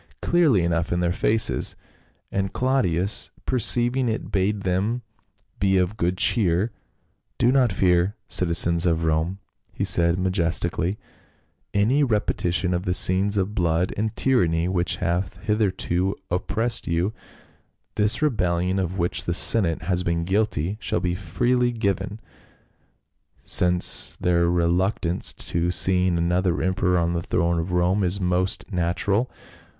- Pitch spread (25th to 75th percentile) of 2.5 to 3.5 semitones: Yes, average, 3.2 semitones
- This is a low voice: Yes, very low, 90 Hz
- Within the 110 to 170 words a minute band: Yes, average, 140 wpm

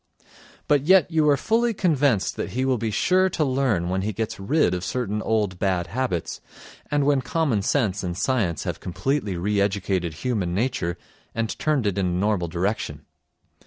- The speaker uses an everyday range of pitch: No, wide, 6.8 semitones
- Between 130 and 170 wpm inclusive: No, average, 180 wpm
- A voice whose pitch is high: No, low, 110 Hz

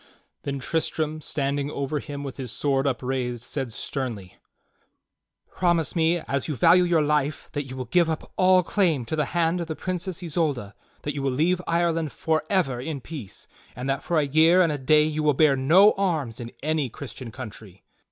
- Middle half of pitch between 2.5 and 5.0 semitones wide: Yes, average, 3.7 semitones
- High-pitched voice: No, medium, 150 Hz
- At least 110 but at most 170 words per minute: No, average, 190 wpm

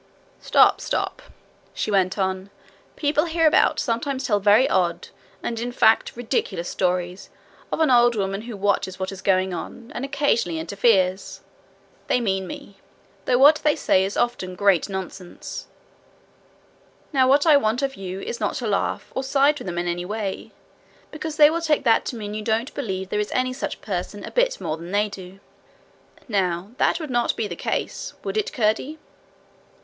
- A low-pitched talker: No, high, 215 Hz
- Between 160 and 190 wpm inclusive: Yes, average, 180 wpm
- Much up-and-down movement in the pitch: Yes, wide, 5.8 semitones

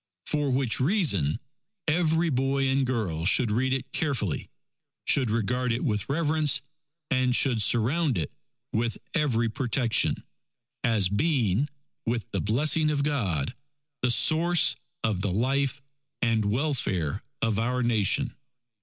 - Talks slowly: Yes, slow, 125 wpm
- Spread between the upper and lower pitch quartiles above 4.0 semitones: Yes, average, 4.7 semitones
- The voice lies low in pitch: Yes, low, 125 Hz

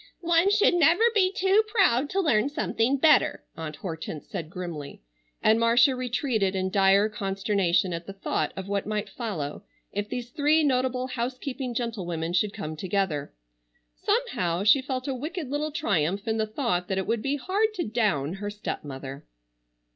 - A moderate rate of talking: Yes, average, 165 wpm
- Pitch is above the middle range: Yes, high, 220 Hz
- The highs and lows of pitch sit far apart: Yes, wide, 6.6 semitones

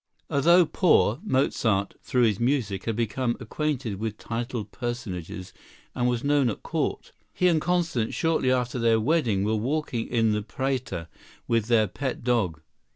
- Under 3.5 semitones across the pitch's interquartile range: No, average, 3.9 semitones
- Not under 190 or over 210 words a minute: No, average, 155 wpm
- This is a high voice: No, low, 120 Hz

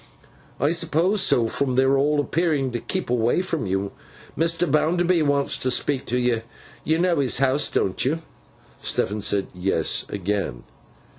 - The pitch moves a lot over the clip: Yes, wide, 5.8 semitones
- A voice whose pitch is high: No, medium, 140 Hz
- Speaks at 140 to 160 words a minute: Yes, average, 155 wpm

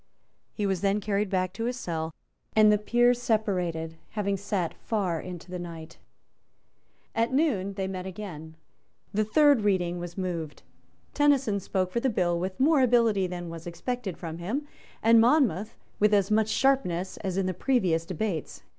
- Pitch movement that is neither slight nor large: Yes, average, 4.4 semitones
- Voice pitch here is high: Yes, high, 195 Hz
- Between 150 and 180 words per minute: Yes, average, 165 wpm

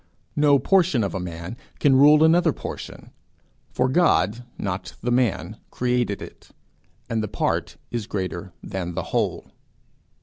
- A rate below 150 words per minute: Yes, average, 140 wpm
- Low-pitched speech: Yes, low, 120 Hz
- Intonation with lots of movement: Yes, wide, 6.6 semitones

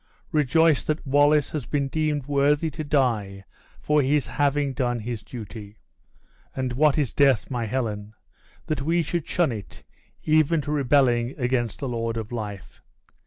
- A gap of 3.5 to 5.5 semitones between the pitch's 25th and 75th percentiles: Yes, average, 4.1 semitones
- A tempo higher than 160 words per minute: No, average, 155 wpm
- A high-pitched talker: No, low, 135 Hz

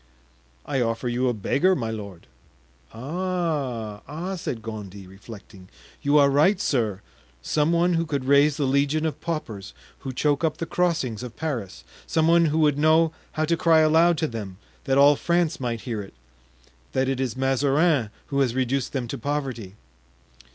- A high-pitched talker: No, medium, 140 Hz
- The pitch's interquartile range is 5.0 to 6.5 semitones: Yes, wide, 5.4 semitones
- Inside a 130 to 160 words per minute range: No, average, 170 wpm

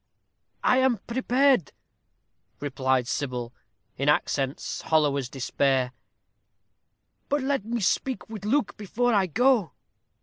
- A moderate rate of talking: No, slow, 110 wpm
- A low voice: No, high, 195 Hz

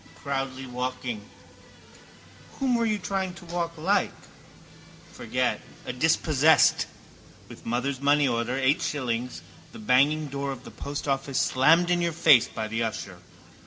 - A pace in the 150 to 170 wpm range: No, average, 140 wpm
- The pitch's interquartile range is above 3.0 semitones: Yes, average, 4.7 semitones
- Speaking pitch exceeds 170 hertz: No, medium, 140 Hz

